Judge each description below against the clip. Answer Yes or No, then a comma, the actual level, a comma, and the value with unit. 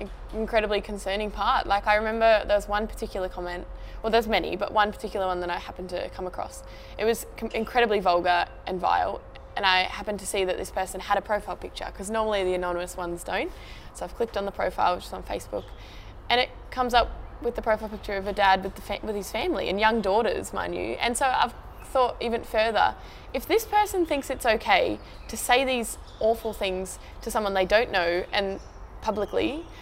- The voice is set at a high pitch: Yes, high, 210 Hz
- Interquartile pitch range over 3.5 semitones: No, average, 2.8 semitones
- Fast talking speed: Yes, fast, 210 wpm